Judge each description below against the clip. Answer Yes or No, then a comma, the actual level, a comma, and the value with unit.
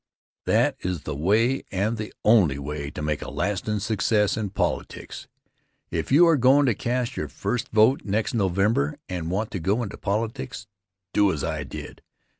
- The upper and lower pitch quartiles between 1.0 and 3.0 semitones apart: No, average, 4.3 semitones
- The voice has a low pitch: Yes, low, 105 Hz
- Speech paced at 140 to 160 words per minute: No, average, 175 wpm